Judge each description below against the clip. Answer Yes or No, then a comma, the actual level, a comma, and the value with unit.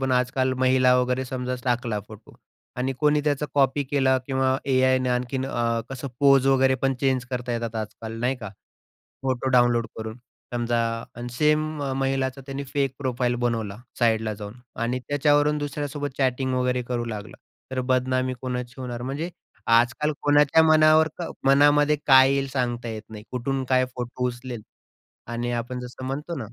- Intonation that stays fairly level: Yes, narrow, 2.1 semitones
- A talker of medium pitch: No, low, 130 Hz